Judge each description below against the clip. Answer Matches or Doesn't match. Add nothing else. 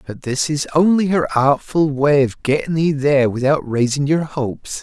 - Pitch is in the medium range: Matches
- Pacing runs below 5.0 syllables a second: Matches